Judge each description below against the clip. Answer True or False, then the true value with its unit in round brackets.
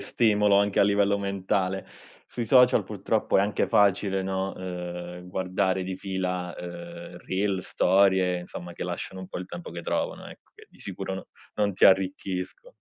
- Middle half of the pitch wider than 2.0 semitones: False (1.7 semitones)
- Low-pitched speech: True (95 Hz)